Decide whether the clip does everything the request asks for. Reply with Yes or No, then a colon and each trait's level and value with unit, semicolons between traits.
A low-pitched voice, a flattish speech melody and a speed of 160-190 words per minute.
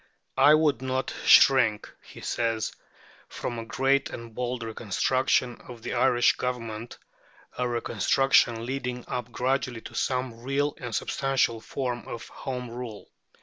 No: low, 125 Hz; narrow, 2.2 semitones; slow, 135 wpm